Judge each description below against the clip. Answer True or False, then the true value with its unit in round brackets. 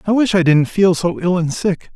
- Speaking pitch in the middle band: True (180 Hz)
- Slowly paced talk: False (275 wpm)